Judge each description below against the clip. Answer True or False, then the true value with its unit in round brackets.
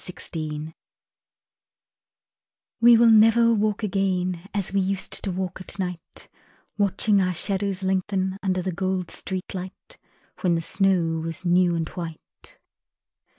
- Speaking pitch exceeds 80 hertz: True (185 Hz)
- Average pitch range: False (2.1 semitones)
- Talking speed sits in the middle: False (130 wpm)